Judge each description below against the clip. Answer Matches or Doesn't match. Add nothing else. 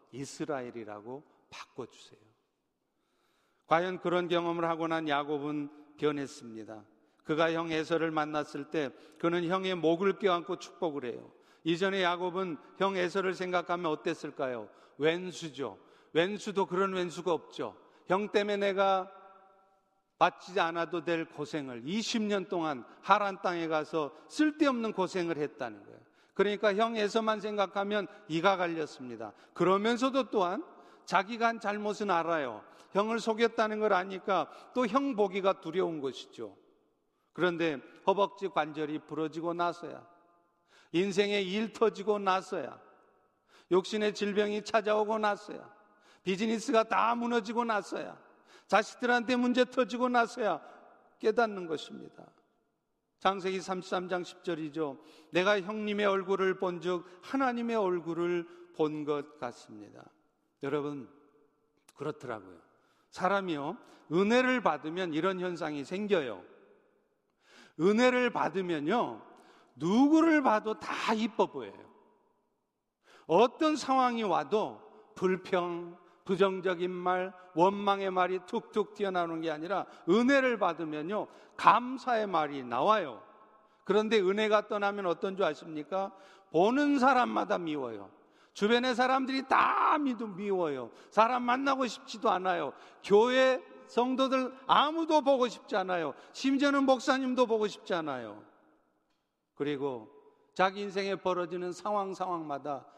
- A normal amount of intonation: Matches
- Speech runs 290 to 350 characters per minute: Doesn't match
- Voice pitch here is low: Doesn't match